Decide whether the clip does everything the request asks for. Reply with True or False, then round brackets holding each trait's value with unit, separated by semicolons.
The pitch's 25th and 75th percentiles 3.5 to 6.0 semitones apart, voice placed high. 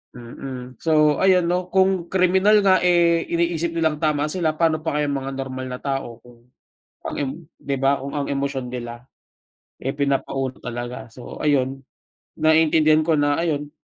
False (3.9 semitones; 145 Hz)